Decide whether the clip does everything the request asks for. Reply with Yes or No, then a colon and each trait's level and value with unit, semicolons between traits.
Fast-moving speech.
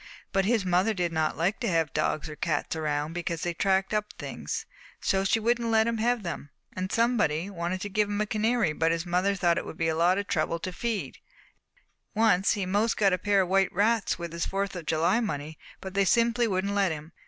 Yes: fast, 235 wpm